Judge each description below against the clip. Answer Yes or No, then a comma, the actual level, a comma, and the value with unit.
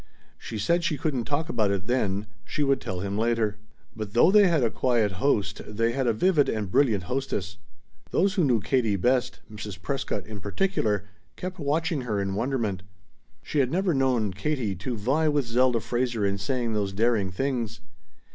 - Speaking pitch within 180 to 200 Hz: No, low, 120 Hz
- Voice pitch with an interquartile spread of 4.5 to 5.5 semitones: Yes, average, 5.2 semitones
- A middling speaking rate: Yes, average, 185 wpm